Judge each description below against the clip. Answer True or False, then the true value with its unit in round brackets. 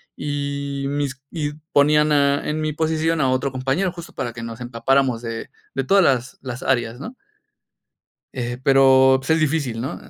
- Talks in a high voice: False (140 Hz)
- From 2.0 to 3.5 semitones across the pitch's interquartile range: True (2.9 semitones)